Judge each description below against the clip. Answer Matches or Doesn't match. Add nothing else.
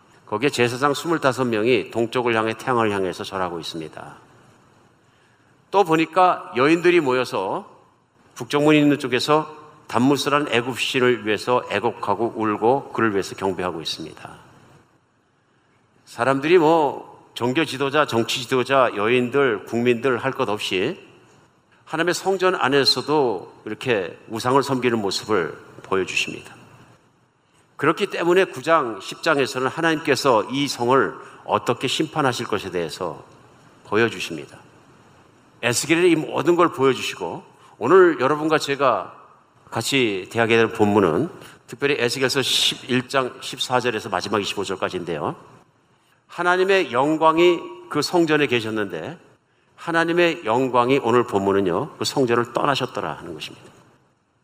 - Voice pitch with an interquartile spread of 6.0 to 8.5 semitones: Doesn't match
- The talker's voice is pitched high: Doesn't match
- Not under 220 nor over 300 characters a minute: Matches